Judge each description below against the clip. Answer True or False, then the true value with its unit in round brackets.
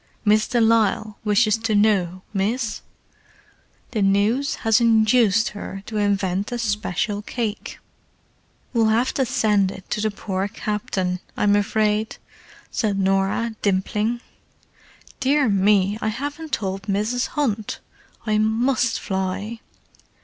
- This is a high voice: True (215 Hz)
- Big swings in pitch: False (2.4 semitones)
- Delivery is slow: True (120 wpm)